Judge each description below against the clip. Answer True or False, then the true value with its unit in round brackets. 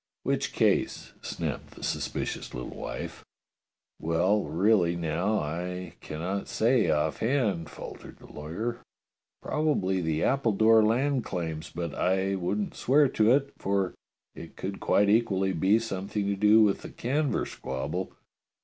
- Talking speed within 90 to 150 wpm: True (140 wpm)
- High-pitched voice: False (100 Hz)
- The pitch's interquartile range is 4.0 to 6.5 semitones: True (4.6 semitones)